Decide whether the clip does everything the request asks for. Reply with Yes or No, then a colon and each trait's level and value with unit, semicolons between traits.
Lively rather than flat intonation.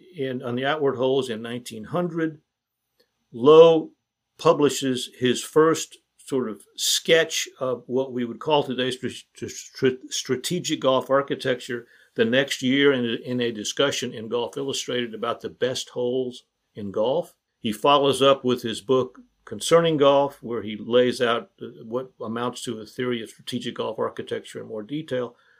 No: average, 3.7 semitones